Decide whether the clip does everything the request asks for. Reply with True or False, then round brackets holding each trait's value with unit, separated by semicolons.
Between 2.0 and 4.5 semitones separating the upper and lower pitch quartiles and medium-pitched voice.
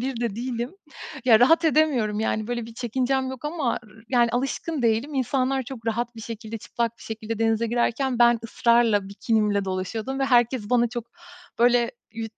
False (2.4 semitones; 235 Hz)